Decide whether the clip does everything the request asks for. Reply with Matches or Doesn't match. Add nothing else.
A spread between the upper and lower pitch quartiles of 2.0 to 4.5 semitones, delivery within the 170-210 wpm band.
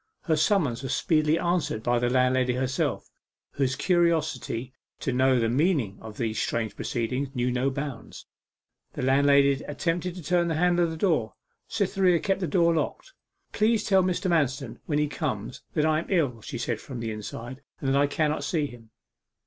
Doesn't match